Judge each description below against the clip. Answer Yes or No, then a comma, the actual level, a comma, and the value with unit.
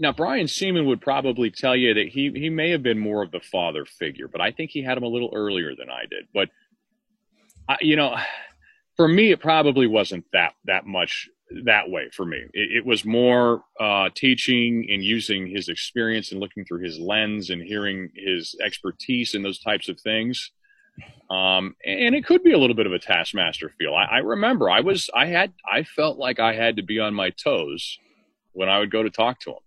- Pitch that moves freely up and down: Yes, wide, 6.9 semitones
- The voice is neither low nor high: No, low, 120 Hz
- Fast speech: Yes, fast, 215 wpm